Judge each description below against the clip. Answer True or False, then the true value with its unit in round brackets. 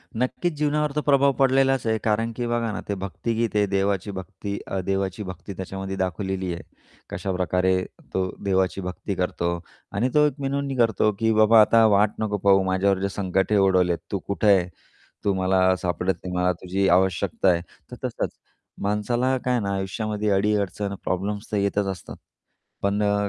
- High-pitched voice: False (100 Hz)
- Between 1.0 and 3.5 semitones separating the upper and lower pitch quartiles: True (2.8 semitones)